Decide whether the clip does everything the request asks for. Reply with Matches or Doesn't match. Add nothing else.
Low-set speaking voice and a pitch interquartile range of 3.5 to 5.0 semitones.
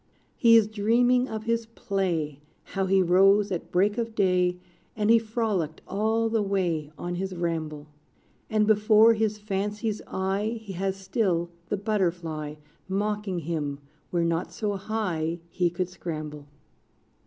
Doesn't match